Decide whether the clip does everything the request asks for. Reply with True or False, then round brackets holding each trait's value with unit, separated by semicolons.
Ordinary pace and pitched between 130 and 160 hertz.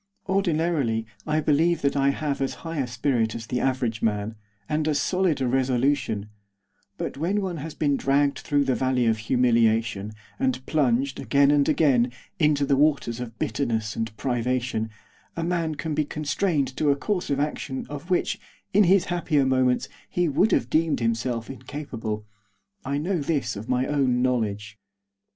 True (170 wpm; 135 Hz)